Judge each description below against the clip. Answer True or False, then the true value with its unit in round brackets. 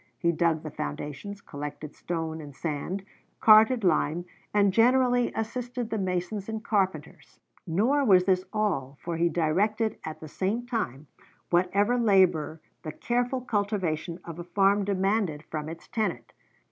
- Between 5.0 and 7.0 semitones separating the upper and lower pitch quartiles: True (5.3 semitones)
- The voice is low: False (190 Hz)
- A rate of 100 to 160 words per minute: True (145 wpm)